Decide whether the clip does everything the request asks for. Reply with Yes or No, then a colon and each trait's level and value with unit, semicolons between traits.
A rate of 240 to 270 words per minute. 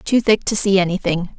No: fast, 215 wpm